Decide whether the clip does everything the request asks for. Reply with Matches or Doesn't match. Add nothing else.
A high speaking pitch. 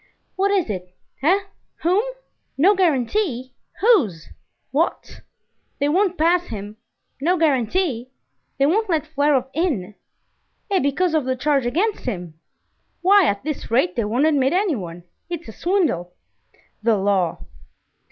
Matches